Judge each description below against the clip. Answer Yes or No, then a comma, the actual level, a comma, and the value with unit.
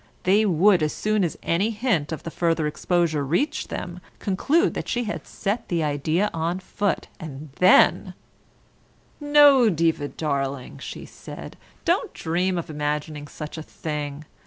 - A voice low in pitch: No, medium, 170 Hz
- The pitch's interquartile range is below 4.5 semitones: No, average, 5.2 semitones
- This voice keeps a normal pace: Yes, average, 150 wpm